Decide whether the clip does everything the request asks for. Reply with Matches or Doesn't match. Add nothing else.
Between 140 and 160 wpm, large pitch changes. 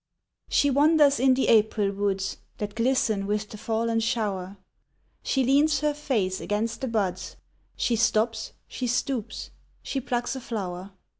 Doesn't match